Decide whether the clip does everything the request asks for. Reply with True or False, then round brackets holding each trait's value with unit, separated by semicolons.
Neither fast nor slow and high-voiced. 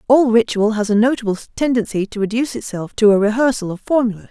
True (195 wpm; 225 Hz)